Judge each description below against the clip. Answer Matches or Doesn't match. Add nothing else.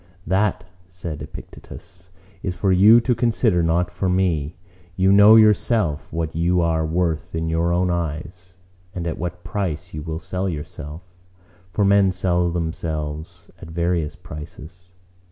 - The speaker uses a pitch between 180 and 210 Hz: Doesn't match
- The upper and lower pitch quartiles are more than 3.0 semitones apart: Doesn't match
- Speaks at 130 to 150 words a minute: Matches